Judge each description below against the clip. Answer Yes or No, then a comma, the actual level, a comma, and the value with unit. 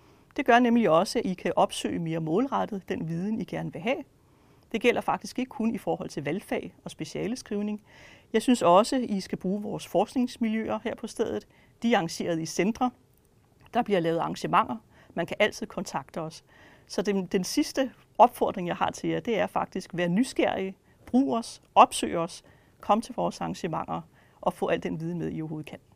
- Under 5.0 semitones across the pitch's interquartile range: No, wide, 5.6 semitones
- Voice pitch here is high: Yes, high, 205 Hz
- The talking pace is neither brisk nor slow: Yes, average, 195 wpm